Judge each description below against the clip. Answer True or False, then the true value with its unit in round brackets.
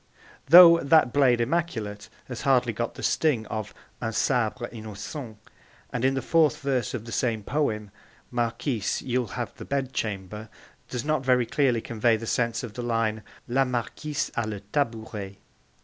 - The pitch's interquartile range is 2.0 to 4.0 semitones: True (3.5 semitones)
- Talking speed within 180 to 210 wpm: False (165 wpm)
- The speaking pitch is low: True (120 Hz)